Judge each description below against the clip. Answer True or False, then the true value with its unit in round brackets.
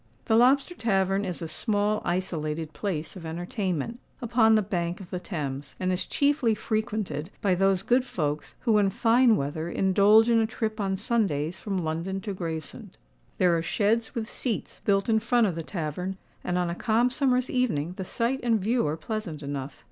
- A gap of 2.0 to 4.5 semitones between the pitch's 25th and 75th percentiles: False (4.9 semitones)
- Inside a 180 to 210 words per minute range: True (185 wpm)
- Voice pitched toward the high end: True (195 Hz)